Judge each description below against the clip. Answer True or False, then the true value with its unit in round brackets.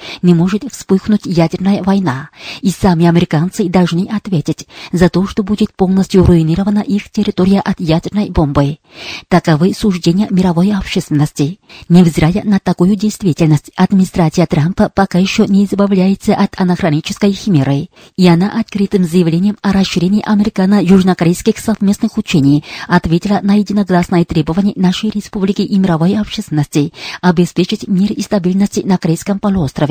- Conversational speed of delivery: True (125 wpm)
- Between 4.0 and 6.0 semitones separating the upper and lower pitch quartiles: False (2.9 semitones)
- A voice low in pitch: False (190 Hz)